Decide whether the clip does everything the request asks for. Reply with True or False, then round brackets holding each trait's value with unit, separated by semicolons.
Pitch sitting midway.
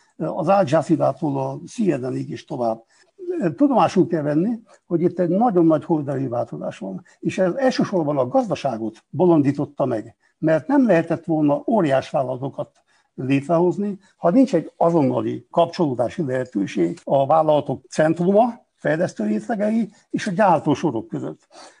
True (165 Hz)